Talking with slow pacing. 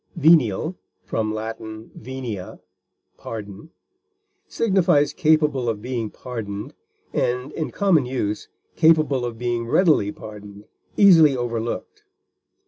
Yes: slow, 95 wpm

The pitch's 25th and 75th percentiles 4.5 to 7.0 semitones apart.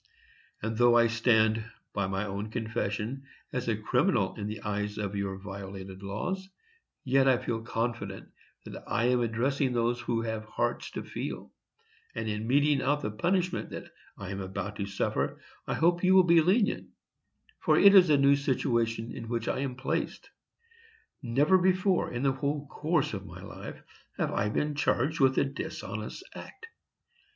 Yes: average, 5.1 semitones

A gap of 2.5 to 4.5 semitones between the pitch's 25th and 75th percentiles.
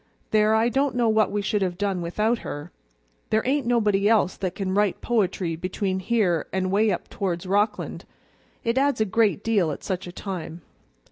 Yes: average, 3.2 semitones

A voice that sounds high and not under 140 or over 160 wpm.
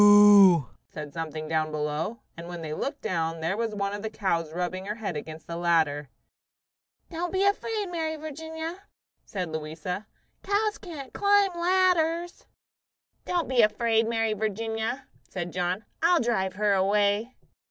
Yes: high, 210 Hz; average, 145 wpm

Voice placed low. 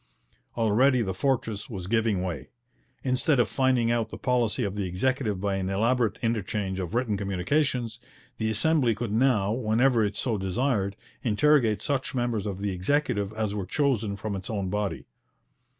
Yes: low, 110 Hz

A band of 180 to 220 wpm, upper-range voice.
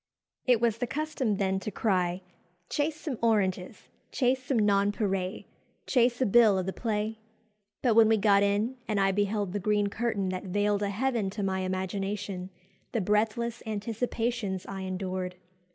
No: average, 160 wpm; high, 205 Hz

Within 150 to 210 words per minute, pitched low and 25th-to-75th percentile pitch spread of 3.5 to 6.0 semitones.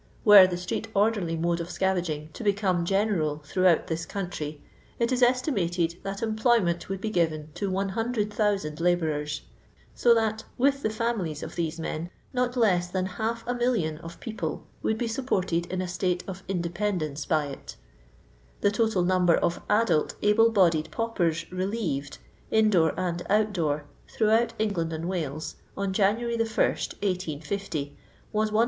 No: average, 160 wpm; high, 190 Hz; average, 4.6 semitones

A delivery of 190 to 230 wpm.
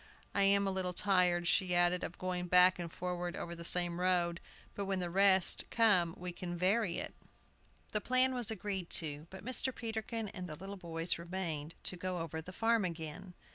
Yes: average, 195 wpm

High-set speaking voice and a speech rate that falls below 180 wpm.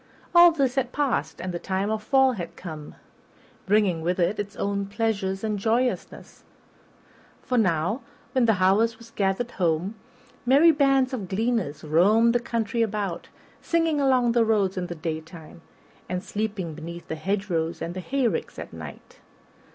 Yes: high, 205 Hz; average, 160 wpm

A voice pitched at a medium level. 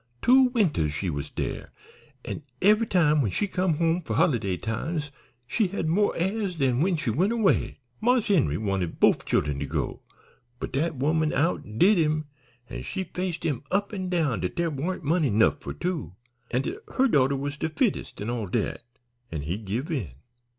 Yes: medium, 155 Hz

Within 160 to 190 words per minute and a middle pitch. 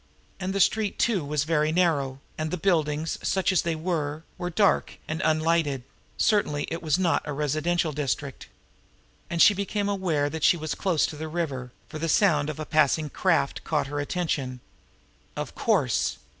Yes: average, 180 wpm; medium, 155 Hz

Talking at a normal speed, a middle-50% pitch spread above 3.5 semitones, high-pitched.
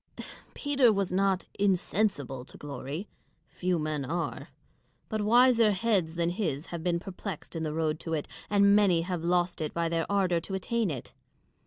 No: average, 170 wpm; average, 3.9 semitones; medium, 180 Hz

